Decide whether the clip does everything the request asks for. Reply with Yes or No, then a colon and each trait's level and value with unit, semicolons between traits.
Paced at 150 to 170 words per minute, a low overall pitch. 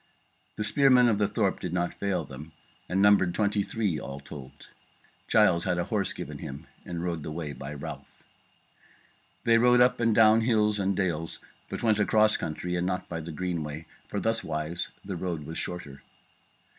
No: average, 185 wpm; very low, 90 Hz